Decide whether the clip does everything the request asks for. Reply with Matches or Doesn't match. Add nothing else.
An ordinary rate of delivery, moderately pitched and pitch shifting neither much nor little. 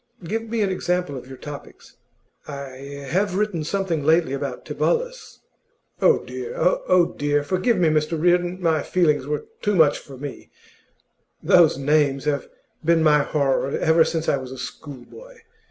Matches